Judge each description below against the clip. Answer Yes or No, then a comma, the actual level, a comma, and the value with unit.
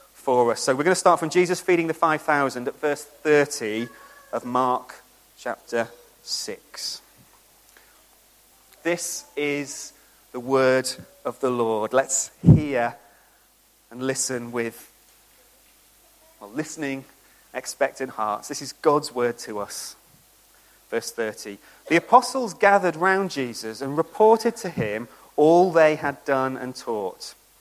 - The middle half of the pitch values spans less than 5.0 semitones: No, wide, 5.4 semitones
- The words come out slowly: Yes, slow, 130 wpm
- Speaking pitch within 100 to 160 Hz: Yes, medium, 140 Hz